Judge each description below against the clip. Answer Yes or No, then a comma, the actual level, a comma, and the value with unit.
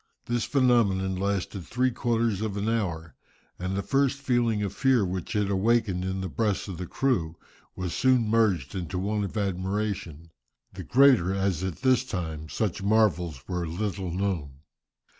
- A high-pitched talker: No, low, 100 Hz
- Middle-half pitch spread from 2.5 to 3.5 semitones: No, average, 4.0 semitones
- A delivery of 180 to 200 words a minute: No, average, 160 wpm